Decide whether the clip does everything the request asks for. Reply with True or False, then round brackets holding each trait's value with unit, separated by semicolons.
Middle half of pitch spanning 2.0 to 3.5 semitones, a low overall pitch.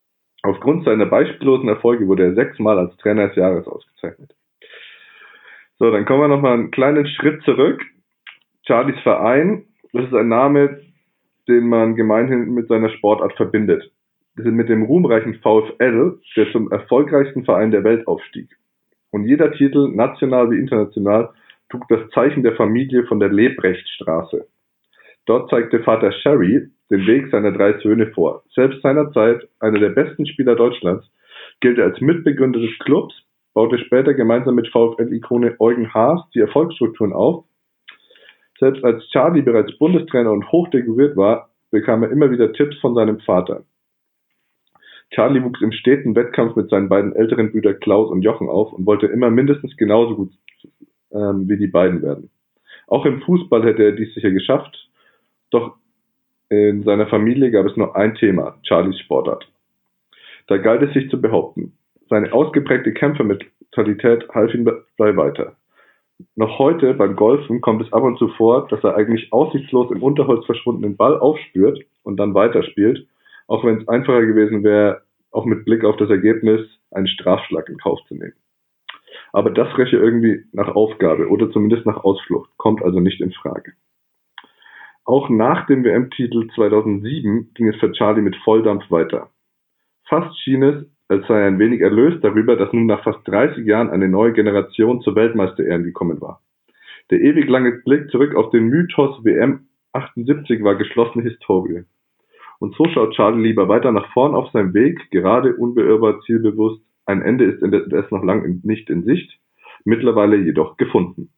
False (4.3 semitones; 115 Hz)